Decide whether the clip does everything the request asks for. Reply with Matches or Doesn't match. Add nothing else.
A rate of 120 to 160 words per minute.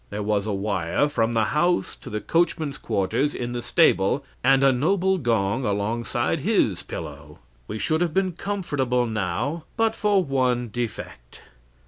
Matches